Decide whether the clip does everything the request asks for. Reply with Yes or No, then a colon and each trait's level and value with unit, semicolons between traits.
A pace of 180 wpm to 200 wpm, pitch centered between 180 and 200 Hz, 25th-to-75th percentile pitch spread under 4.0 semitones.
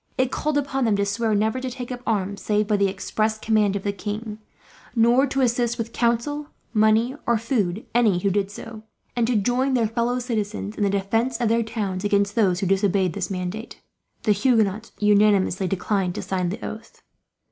No: average, 195 wpm; high, 215 Hz; average, 2.8 semitones